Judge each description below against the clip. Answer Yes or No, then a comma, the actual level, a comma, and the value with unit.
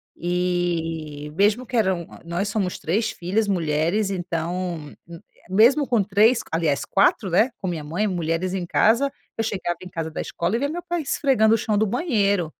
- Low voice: No, medium, 185 Hz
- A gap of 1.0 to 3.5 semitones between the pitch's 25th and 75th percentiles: No, average, 4.4 semitones